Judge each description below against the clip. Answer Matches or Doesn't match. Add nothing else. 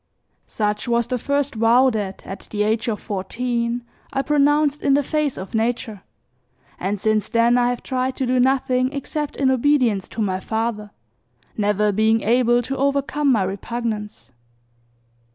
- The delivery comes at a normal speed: Matches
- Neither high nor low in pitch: Doesn't match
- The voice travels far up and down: Doesn't match